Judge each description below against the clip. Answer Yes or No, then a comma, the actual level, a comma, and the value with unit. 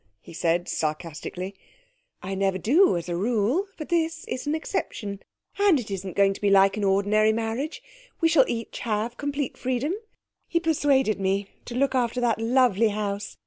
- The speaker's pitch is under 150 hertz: No, high, 225 Hz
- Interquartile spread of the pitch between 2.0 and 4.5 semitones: No, wide, 5.5 semitones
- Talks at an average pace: Yes, average, 175 wpm